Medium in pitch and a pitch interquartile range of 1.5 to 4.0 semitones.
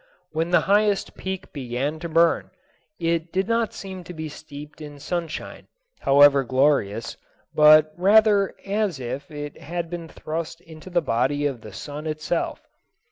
Yes: medium, 155 Hz; average, 3.5 semitones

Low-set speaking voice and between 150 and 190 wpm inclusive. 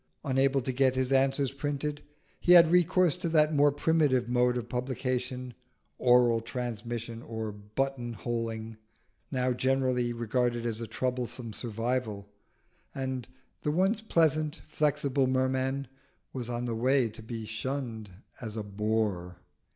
No: low, 125 Hz; slow, 135 wpm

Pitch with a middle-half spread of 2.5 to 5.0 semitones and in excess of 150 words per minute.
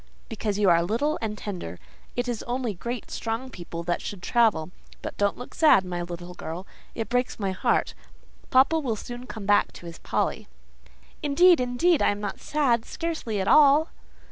No: wide, 5.4 semitones; average, 180 wpm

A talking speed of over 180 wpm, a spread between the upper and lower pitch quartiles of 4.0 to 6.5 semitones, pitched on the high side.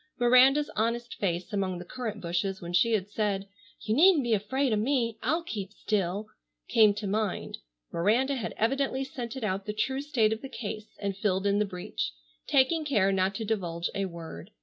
Yes: average, 190 wpm; average, 4.3 semitones; high, 215 Hz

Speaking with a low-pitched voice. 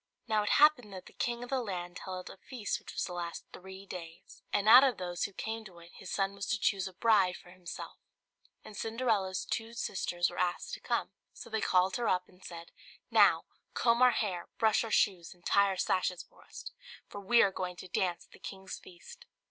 No: high, 190 Hz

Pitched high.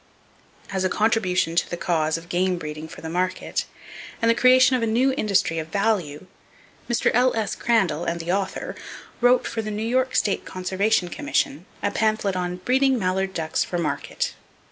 Yes: high, 195 Hz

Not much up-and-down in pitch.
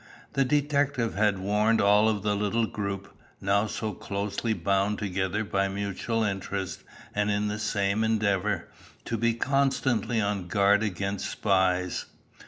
Yes: narrow, 2.0 semitones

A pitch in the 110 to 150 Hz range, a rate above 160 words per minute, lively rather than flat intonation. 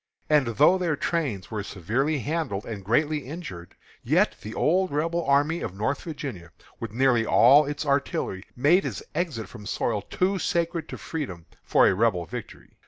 Yes: medium, 140 Hz; average, 170 wpm; wide, 7.1 semitones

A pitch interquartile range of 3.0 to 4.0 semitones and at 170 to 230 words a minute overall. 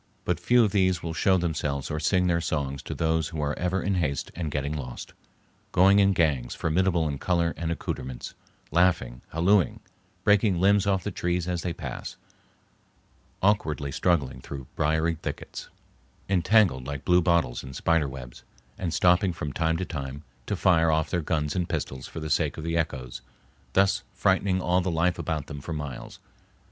Yes: average, 3.6 semitones; average, 175 wpm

